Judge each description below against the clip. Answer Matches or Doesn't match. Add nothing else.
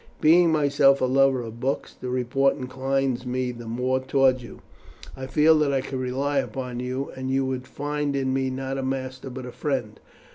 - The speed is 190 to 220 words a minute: Matches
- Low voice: Matches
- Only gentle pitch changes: Matches